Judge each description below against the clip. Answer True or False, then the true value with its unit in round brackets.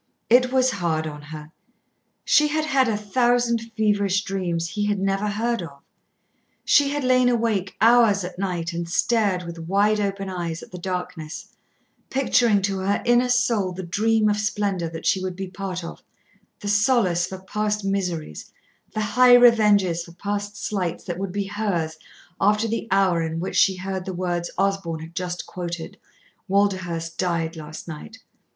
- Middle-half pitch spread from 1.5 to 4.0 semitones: True (3.6 semitones)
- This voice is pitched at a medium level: False (195 Hz)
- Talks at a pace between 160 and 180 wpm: True (170 wpm)